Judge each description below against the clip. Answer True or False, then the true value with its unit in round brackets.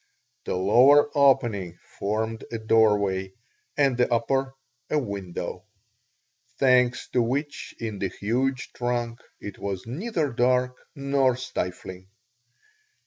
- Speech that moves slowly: True (110 wpm)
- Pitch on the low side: True (120 Hz)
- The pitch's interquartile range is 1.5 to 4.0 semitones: False (4.7 semitones)